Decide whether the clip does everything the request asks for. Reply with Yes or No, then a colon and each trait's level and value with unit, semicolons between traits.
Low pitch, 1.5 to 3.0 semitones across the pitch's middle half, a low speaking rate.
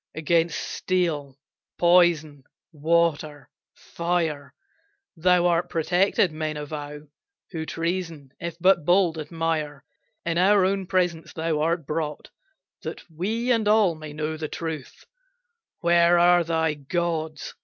No: medium, 165 Hz; narrow, 2.4 semitones; slow, 120 wpm